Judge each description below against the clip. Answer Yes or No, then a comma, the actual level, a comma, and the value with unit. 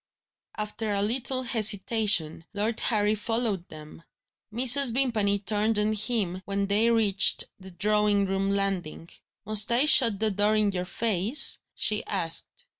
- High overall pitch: Yes, high, 210 Hz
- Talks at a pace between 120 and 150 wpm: Yes, average, 140 wpm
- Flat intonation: Yes, narrow, 2.3 semitones